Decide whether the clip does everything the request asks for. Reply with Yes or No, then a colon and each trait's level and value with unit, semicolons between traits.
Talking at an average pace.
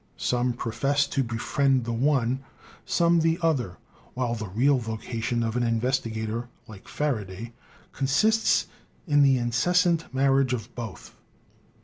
No: slow, 125 wpm